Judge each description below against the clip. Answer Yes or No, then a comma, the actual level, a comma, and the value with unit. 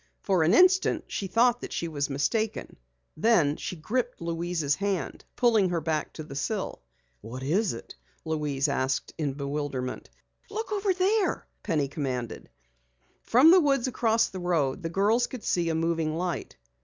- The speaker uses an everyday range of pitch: No, wide, 7.5 semitones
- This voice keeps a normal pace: Yes, average, 160 wpm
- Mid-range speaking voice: Yes, medium, 170 Hz